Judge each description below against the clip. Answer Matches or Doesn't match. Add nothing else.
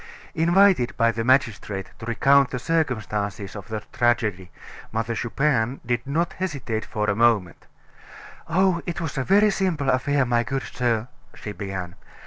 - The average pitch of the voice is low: Matches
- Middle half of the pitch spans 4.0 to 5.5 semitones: Matches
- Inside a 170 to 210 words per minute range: Doesn't match